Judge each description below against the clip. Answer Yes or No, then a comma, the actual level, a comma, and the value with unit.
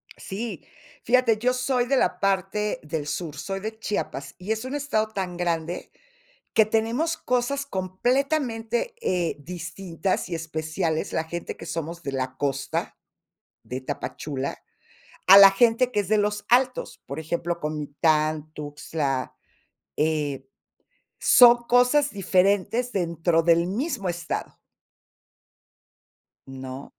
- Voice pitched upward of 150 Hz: Yes, medium, 185 Hz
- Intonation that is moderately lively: No, wide, 6.4 semitones